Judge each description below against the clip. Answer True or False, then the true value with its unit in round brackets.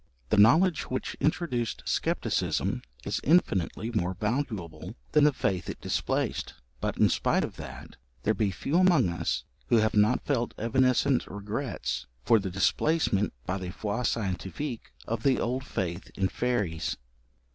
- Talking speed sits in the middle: True (145 wpm)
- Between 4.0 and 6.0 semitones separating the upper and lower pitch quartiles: True (5.4 semitones)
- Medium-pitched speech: False (110 Hz)